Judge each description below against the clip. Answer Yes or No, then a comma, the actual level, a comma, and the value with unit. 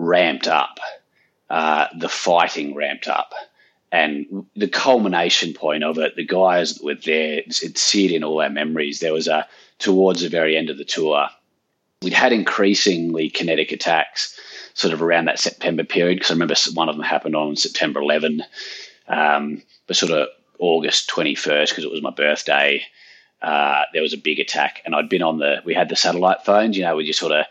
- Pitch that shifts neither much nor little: Yes, average, 3.6 semitones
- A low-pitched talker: Yes, very low, 80 Hz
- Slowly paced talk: No, average, 190 wpm